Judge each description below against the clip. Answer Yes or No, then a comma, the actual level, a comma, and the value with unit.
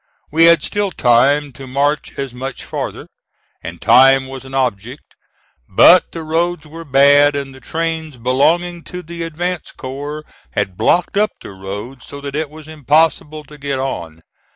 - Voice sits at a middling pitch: Yes, medium, 145 Hz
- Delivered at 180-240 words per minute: No, average, 165 wpm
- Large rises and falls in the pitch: No, average, 3.5 semitones